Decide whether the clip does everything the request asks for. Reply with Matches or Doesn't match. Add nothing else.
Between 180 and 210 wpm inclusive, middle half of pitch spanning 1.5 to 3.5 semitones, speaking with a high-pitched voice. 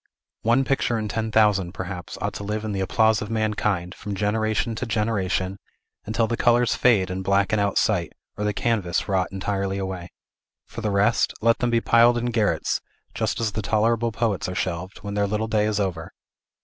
Doesn't match